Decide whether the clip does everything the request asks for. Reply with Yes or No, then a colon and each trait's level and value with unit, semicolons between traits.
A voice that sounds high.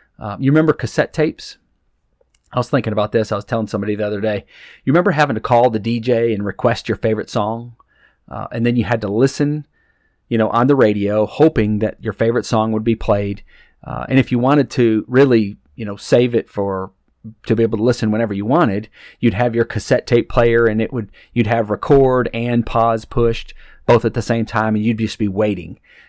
No: low, 115 Hz